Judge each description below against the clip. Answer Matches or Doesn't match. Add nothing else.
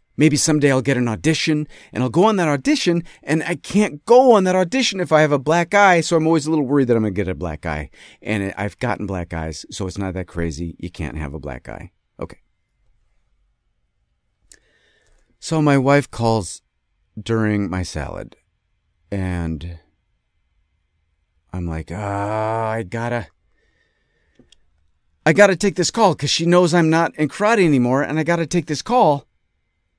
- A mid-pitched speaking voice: Doesn't match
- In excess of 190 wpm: Doesn't match